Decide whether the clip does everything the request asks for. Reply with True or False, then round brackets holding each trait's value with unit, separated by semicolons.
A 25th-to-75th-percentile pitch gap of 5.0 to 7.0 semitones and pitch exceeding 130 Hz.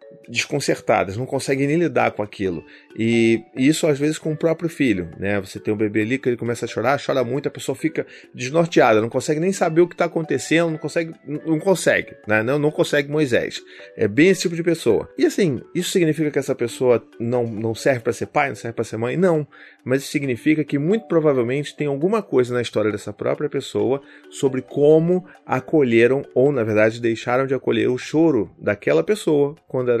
True (5.3 semitones; 140 Hz)